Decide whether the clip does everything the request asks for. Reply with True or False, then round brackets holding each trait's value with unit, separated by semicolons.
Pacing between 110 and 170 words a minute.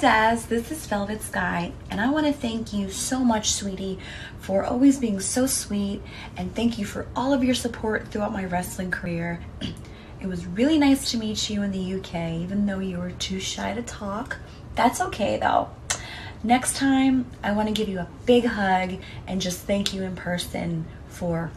False (190 wpm)